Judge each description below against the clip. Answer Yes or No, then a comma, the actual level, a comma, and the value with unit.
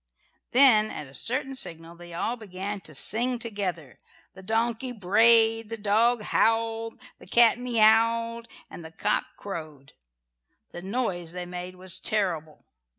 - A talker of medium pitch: No, high, 215 Hz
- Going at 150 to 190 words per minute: No, average, 140 wpm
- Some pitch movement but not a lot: Yes, average, 4.6 semitones